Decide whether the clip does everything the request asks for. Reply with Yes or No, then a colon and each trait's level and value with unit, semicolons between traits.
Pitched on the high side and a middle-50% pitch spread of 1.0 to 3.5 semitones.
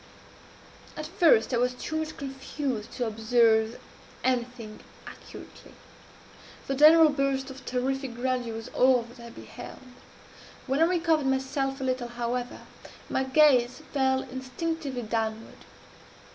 Yes: very high, 260 Hz; narrow, 2.5 semitones